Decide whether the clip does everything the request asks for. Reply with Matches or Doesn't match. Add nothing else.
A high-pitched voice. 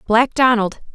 Matches